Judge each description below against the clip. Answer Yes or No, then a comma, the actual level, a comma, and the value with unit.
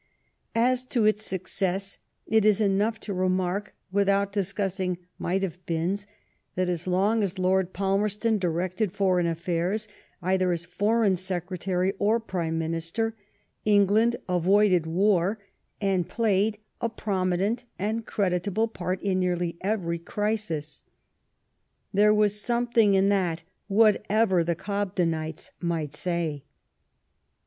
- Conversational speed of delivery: No, slow, 120 wpm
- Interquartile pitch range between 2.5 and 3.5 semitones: Yes, average, 2.9 semitones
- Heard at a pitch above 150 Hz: Yes, high, 190 Hz